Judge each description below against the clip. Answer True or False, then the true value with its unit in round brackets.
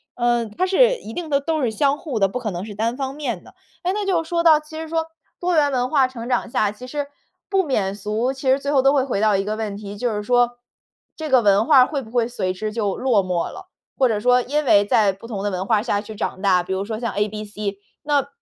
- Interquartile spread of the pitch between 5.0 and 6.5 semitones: True (5.3 semitones)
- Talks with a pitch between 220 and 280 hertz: True (240 Hz)